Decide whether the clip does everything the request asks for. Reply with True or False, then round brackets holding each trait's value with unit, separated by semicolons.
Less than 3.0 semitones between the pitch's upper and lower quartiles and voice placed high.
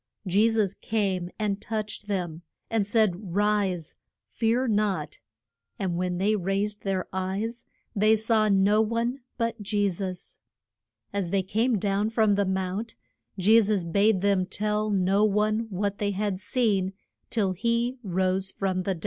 True (2.4 semitones; 205 Hz)